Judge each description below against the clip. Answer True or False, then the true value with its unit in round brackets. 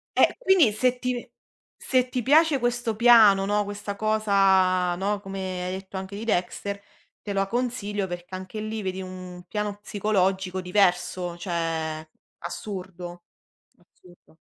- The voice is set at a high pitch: True (195 Hz)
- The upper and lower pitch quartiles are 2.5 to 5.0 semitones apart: True (2.9 semitones)